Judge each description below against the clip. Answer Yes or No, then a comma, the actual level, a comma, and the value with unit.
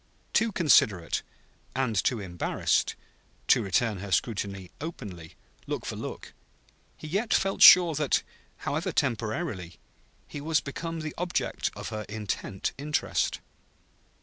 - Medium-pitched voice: No, low, 120 Hz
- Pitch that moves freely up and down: Yes, wide, 8.4 semitones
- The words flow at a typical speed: No, slow, 120 wpm